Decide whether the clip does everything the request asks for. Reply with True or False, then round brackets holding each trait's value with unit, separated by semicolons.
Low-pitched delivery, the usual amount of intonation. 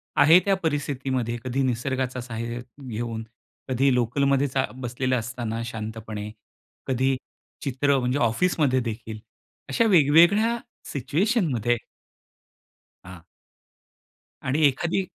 True (130 Hz; 3.4 semitones)